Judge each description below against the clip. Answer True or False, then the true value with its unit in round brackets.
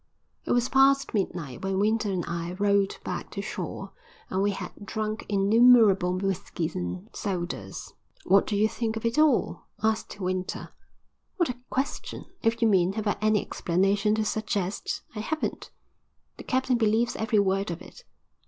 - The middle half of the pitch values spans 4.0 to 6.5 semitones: False (3.2 semitones)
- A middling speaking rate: True (160 wpm)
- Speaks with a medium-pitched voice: False (205 Hz)